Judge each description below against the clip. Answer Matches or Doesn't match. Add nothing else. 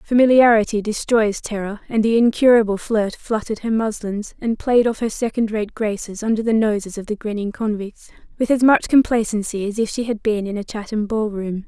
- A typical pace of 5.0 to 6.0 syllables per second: Matches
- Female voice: Matches